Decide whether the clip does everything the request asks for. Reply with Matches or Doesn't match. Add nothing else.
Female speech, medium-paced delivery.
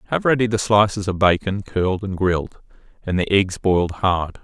Doesn't match